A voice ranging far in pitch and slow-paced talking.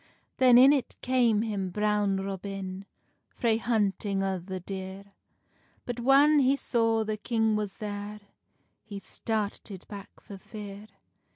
No: average, 2.7 semitones; slow, 130 wpm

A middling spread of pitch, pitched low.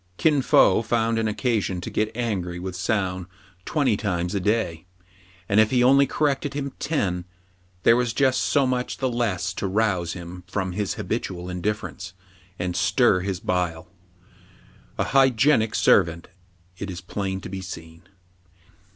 Yes: average, 5.0 semitones; low, 100 Hz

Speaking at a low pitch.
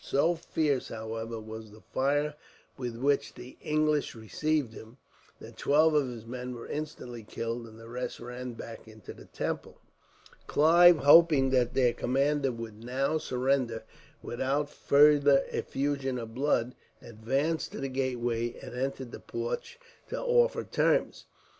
Yes: low, 130 Hz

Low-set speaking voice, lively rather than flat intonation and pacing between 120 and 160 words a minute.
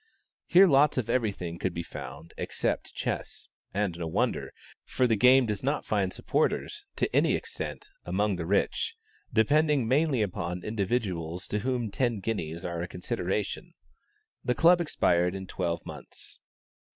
Yes: low, 105 Hz; wide, 6.1 semitones; average, 150 wpm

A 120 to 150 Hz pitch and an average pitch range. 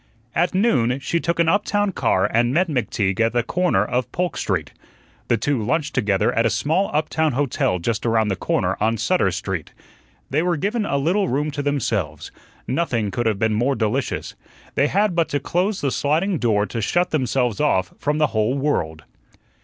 No: low, 135 Hz; wide, 7.0 semitones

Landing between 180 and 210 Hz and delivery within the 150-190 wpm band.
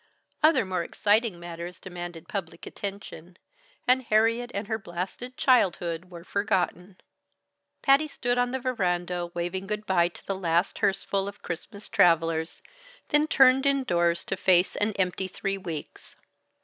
No: high, 190 Hz; average, 140 wpm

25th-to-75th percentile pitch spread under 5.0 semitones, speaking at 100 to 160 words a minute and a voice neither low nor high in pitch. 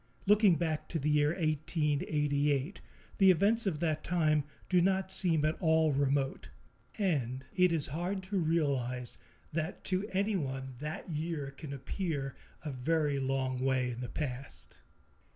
Yes: average, 4.2 semitones; average, 145 wpm; medium, 155 Hz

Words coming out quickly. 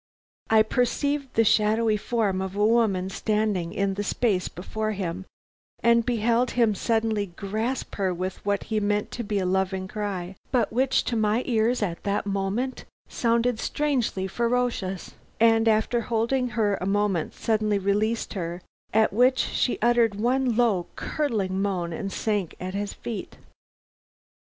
No: average, 150 wpm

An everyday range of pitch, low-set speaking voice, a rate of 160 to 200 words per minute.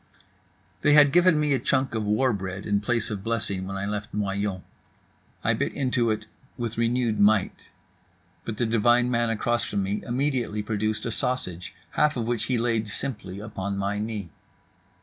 Yes: average, 3.1 semitones; low, 110 Hz; average, 175 wpm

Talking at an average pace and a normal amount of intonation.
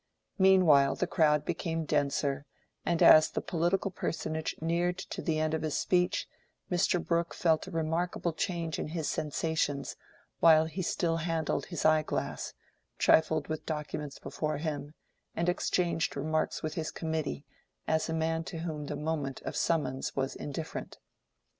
No: average, 150 wpm; narrow, 1.9 semitones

